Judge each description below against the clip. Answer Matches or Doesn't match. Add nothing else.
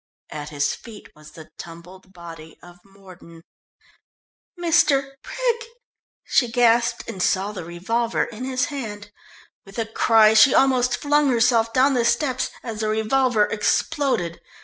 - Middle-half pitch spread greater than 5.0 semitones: Matches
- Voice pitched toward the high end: Matches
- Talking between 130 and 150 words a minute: Matches